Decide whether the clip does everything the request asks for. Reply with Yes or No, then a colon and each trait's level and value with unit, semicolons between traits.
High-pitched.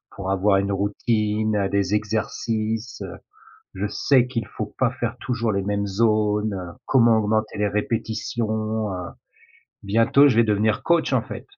No: low, 110 Hz